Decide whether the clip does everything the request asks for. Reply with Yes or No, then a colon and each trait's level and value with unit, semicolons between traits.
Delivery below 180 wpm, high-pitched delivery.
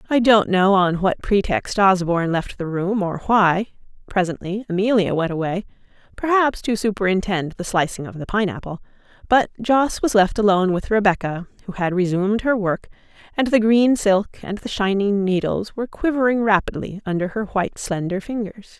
Yes: average, 170 wpm; high, 200 Hz